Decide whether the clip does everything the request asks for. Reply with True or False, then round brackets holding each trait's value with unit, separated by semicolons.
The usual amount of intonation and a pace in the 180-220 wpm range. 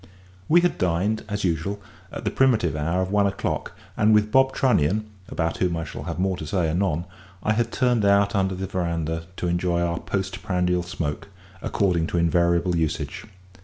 True (3.3 semitones; 185 wpm)